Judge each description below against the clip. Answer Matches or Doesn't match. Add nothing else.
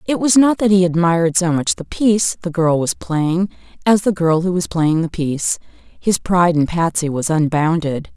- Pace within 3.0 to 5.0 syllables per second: Matches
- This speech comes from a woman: Matches